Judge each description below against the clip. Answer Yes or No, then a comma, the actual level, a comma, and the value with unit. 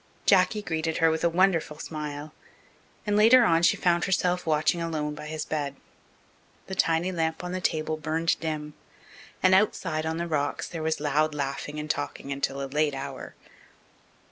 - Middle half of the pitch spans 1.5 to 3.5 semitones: Yes, narrow, 2.4 semitones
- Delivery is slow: No, average, 170 wpm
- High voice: No, medium, 160 Hz